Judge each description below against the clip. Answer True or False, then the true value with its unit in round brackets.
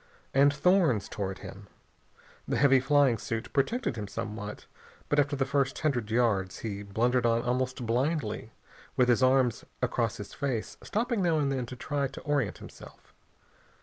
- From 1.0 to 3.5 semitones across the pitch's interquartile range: False (3.9 semitones)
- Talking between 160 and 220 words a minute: True (165 wpm)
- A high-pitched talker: False (125 Hz)